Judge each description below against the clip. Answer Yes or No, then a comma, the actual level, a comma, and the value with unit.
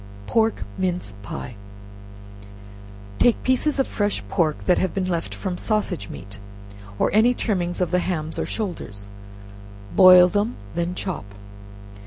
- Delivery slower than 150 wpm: Yes, slow, 135 wpm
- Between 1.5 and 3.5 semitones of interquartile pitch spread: No, average, 3.9 semitones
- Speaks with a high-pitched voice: No, medium, 180 Hz